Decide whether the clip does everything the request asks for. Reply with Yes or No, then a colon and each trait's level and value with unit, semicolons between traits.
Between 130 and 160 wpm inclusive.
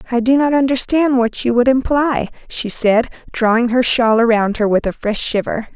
No: average, 200 wpm